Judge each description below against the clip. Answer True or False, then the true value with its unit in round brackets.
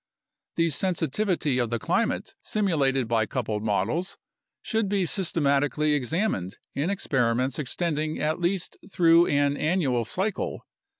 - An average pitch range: False (5.8 semitones)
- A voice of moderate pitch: True (150 Hz)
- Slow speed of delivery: True (120 wpm)